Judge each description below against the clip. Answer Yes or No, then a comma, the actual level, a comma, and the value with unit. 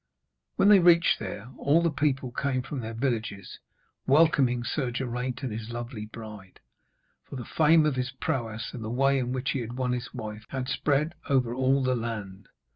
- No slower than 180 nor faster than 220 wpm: Yes, average, 190 wpm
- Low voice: Yes, low, 125 Hz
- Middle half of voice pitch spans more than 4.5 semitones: No, average, 3.1 semitones